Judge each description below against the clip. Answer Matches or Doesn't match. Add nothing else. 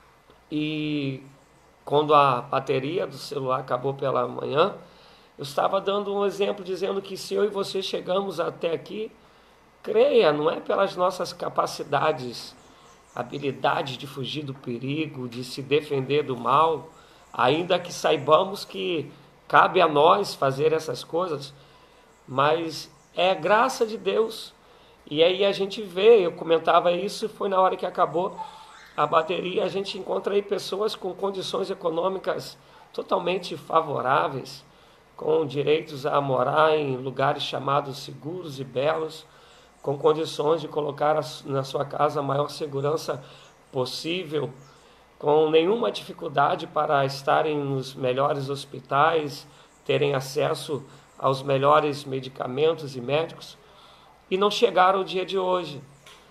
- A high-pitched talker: Doesn't match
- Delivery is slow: Doesn't match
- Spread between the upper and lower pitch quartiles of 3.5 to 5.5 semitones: Matches